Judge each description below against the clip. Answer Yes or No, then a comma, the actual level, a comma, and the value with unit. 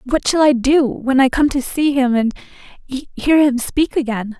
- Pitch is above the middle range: Yes, very high, 270 Hz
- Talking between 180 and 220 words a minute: Yes, fast, 205 wpm